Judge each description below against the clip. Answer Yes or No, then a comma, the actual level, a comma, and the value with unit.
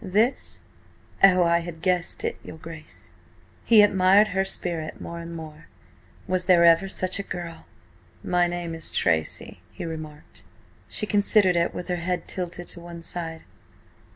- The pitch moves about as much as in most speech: No, narrow, 1.9 semitones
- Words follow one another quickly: No, average, 155 wpm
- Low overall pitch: No, medium, 175 Hz